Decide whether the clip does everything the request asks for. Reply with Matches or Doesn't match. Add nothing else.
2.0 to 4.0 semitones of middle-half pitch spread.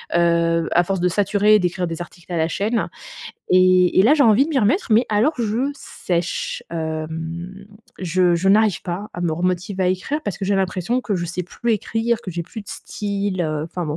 Matches